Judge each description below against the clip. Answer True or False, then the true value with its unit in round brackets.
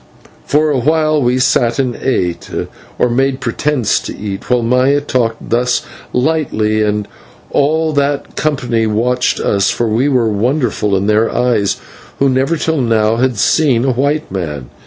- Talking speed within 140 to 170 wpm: True (155 wpm)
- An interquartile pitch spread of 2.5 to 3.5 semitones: False (4.2 semitones)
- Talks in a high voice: False (125 Hz)